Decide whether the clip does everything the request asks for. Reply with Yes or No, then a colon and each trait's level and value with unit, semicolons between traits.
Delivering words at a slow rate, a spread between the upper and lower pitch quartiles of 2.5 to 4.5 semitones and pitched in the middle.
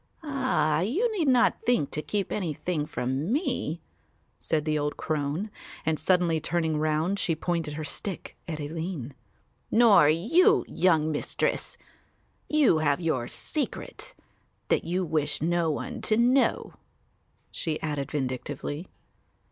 No: slow, 130 wpm; average, 4.9 semitones; medium, 160 Hz